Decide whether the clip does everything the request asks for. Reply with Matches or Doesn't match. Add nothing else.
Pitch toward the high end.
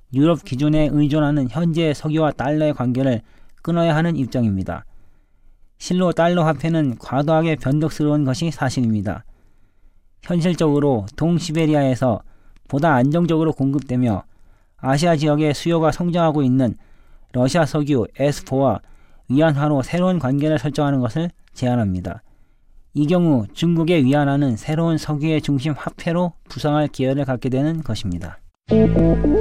Doesn't match